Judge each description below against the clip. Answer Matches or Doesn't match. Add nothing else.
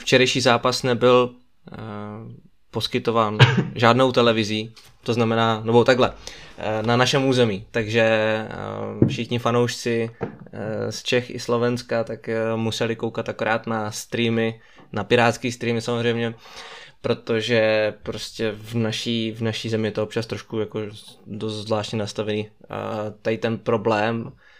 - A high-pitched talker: Doesn't match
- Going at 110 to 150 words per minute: Matches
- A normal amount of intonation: Doesn't match